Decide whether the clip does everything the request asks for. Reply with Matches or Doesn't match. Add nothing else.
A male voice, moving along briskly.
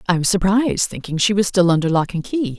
Doesn't match